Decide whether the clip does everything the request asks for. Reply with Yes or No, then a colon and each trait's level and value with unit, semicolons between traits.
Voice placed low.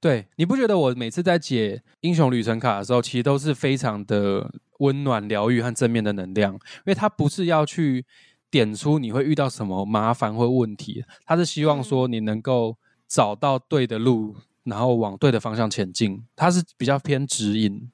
Yes: low, 125 Hz